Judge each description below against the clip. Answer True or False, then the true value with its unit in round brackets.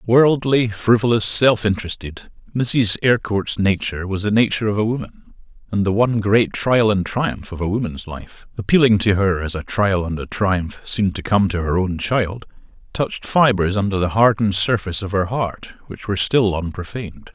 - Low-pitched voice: True (100 Hz)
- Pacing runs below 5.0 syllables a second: False (5.1 syllables/s)